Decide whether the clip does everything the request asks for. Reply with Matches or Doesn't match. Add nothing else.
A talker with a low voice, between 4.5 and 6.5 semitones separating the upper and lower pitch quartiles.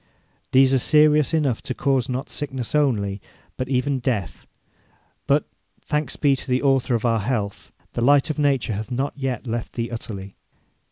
Doesn't match